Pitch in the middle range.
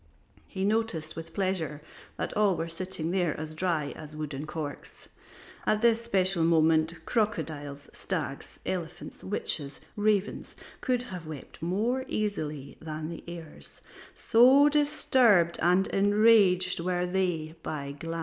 Yes: medium, 175 Hz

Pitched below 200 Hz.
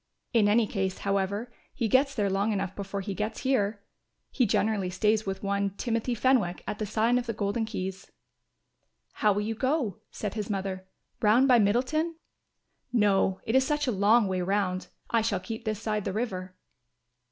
No: high, 210 Hz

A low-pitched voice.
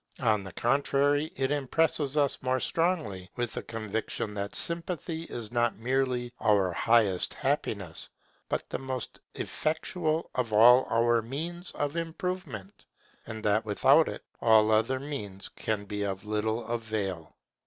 Yes: low, 120 Hz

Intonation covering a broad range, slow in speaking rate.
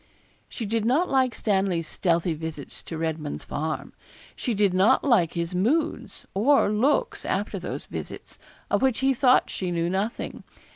No: wide, 6.9 semitones; average, 155 wpm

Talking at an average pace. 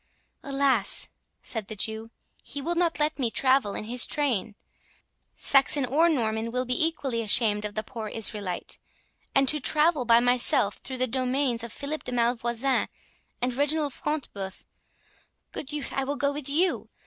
Yes: average, 160 wpm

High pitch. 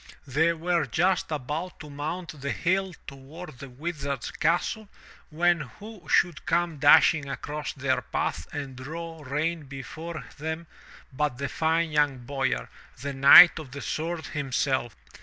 No: medium, 150 Hz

